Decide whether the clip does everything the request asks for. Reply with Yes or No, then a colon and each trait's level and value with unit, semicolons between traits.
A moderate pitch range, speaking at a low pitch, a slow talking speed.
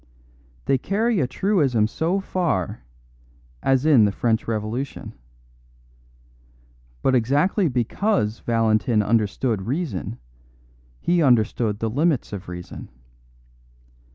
No: wide, 6.8 semitones; low, 125 Hz; slow, 100 wpm